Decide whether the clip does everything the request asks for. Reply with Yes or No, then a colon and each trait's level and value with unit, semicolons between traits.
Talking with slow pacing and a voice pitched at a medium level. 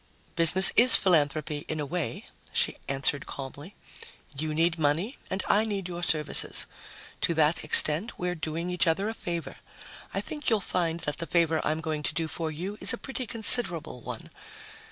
No: average, 175 wpm; medium, 165 Hz